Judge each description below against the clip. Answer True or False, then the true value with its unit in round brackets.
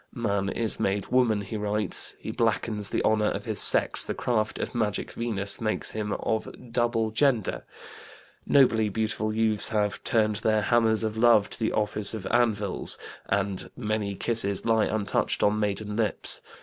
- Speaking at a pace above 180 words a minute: False (160 wpm)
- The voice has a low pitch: True (110 Hz)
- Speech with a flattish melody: True (1.5 semitones)